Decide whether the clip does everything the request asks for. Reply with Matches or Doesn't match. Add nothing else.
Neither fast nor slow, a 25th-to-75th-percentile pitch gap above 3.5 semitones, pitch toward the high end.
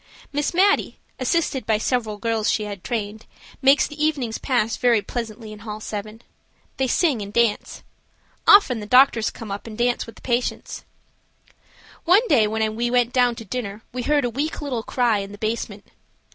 Doesn't match